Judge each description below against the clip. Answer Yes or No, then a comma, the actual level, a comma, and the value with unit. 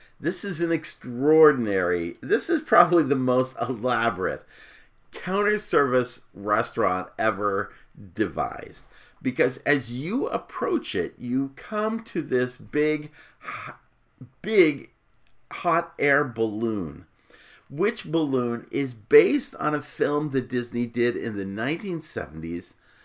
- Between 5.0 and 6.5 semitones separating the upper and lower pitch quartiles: Yes, wide, 5.6 semitones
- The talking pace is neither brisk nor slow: No, slow, 110 wpm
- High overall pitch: No, medium, 140 Hz